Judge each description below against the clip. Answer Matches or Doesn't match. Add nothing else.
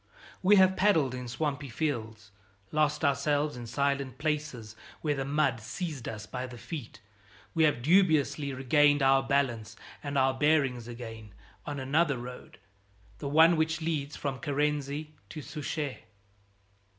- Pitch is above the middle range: Doesn't match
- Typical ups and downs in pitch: Matches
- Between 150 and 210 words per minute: Doesn't match